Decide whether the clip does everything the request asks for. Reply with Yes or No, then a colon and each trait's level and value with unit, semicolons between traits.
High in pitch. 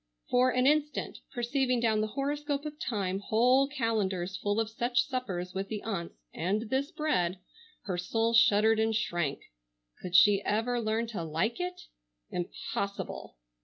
Yes: high, 225 Hz